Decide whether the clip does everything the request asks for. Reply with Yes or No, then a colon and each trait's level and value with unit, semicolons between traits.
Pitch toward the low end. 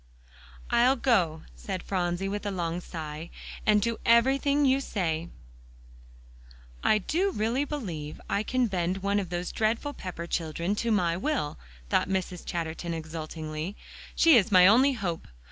No: high, 190 Hz